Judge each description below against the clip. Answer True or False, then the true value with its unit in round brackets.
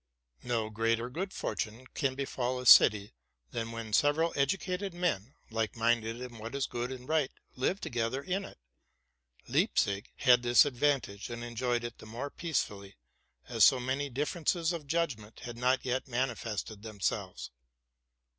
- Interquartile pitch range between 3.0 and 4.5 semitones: True (3.7 semitones)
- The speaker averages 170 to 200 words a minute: False (155 wpm)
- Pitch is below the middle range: True (125 Hz)